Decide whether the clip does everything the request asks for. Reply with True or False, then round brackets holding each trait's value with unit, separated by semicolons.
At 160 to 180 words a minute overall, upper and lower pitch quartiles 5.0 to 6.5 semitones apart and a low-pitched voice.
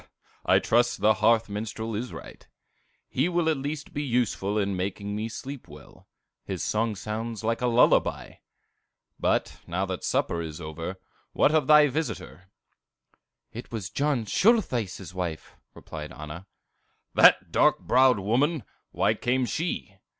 False (145 wpm; 5.4 semitones; 110 Hz)